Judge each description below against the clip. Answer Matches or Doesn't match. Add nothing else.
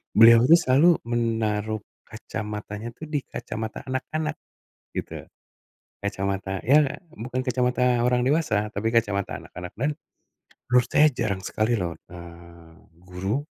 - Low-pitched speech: Matches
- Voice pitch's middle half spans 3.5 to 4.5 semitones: Matches